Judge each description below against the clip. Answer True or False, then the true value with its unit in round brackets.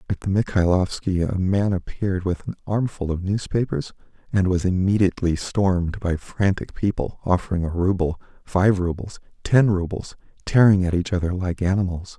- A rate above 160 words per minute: False (155 wpm)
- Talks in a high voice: False (95 Hz)